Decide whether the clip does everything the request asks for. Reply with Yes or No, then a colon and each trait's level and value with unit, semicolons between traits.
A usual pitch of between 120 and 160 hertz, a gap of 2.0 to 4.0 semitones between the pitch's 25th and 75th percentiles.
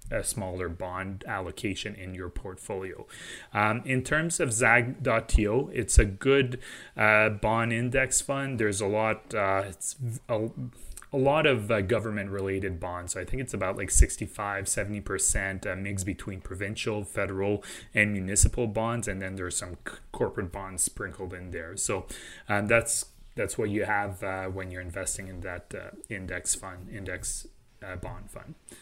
No: low, 100 Hz; average, 3.3 semitones